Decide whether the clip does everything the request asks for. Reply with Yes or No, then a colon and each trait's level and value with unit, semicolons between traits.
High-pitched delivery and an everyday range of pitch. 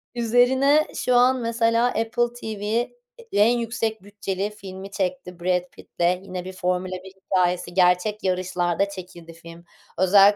Yes: high, 195 Hz; average, 4.2 semitones